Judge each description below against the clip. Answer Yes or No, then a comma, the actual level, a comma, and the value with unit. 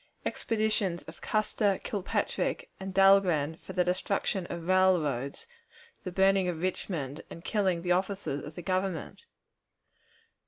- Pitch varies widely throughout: No, narrow, 2.5 semitones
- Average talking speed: No, slow, 125 wpm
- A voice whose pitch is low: No, medium, 185 Hz